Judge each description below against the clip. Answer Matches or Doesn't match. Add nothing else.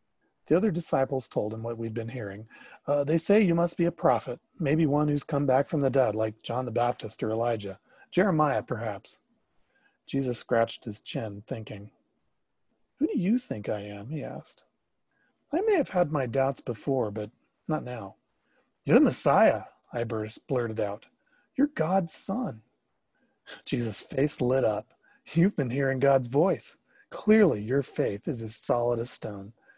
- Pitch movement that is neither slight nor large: Doesn't match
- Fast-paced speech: Doesn't match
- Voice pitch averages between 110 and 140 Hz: Matches